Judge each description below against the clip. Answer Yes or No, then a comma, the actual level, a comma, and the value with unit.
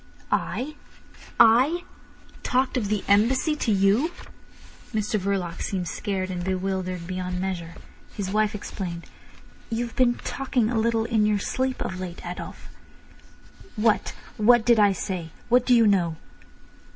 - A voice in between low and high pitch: No, high, 210 Hz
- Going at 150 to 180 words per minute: No, slow, 135 wpm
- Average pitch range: Yes, average, 4.2 semitones